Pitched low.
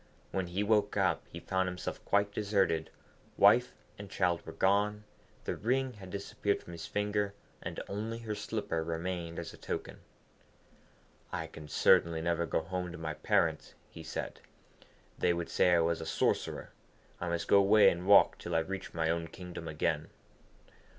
Yes: very low, 90 Hz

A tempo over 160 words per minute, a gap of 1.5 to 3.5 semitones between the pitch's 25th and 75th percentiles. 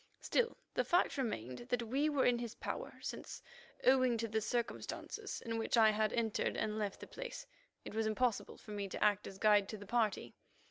Yes: average, 200 wpm; average, 2.9 semitones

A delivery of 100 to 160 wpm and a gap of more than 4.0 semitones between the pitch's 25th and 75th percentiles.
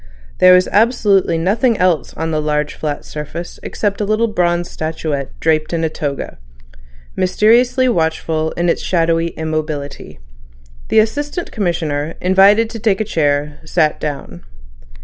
Yes: average, 140 wpm; average, 4.9 semitones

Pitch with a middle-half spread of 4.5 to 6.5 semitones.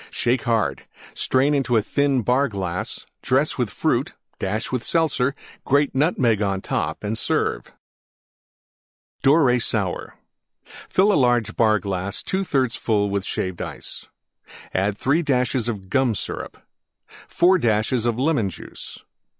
Yes: average, 5.0 semitones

